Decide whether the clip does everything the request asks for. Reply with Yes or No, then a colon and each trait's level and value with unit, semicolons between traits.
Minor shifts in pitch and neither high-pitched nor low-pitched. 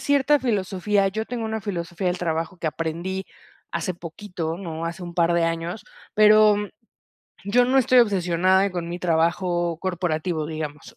No: average, 3.7 semitones; medium, 180 Hz